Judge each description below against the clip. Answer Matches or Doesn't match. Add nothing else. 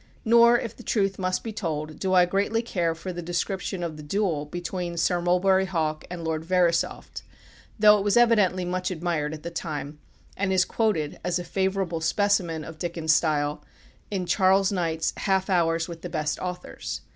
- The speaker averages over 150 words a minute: Matches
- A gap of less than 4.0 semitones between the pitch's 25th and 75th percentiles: Matches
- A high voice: Doesn't match